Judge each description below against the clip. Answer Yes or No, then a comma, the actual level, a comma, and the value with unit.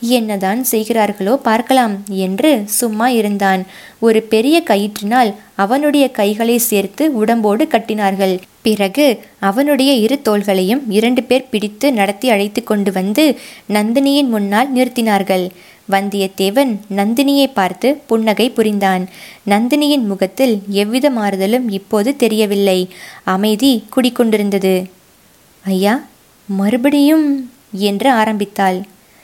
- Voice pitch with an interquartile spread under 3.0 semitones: No, average, 4.2 semitones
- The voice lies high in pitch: Yes, high, 215 Hz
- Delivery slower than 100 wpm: Yes, average, 90 wpm